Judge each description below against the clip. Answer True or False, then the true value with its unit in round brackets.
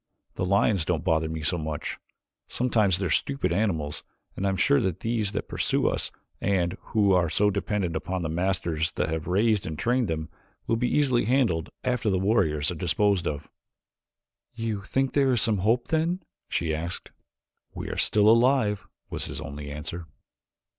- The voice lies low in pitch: True (95 Hz)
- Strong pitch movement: True (5.7 semitones)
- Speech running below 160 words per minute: False (180 wpm)